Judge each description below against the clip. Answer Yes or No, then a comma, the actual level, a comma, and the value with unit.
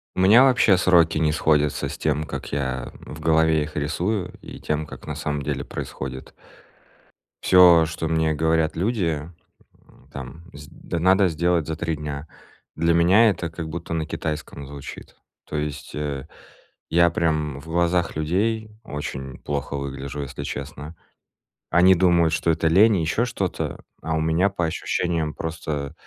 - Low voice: Yes, very low, 80 Hz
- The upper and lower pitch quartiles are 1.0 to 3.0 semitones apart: Yes, average, 2.7 semitones